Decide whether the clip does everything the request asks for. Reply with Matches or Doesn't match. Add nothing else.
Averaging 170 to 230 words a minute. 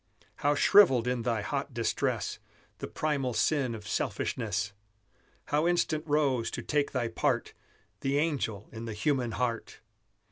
Doesn't match